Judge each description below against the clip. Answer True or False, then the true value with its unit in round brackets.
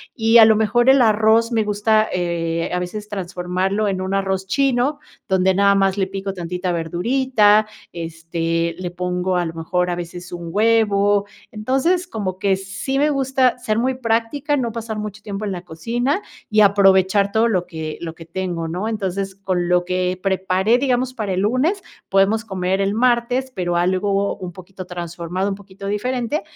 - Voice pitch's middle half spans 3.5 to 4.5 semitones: True (3.9 semitones)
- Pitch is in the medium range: False (195 Hz)